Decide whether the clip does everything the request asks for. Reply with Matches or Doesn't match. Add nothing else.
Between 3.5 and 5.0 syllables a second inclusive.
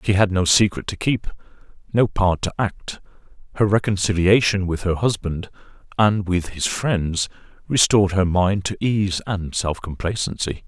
Matches